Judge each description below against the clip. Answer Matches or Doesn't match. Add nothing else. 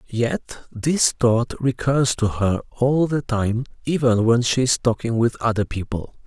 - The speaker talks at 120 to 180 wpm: Matches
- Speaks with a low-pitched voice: Matches